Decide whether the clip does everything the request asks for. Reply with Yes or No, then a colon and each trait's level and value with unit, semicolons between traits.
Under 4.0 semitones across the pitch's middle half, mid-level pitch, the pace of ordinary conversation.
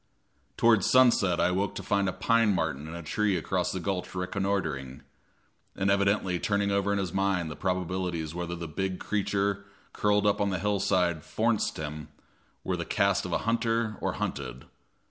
No: average, 2.7 semitones; very low, 95 Hz; average, 175 wpm